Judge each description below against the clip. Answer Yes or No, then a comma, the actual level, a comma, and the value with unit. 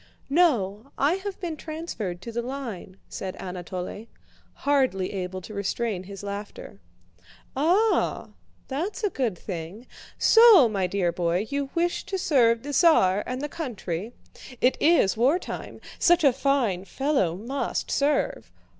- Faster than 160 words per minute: No, slow, 135 wpm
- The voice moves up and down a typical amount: No, wide, 7.5 semitones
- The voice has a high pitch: Yes, high, 240 Hz